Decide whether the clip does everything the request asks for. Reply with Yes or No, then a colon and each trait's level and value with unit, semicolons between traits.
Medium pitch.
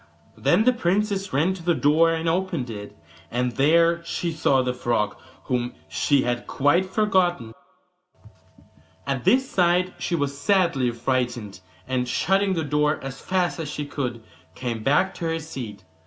Yes: medium, 150 Hz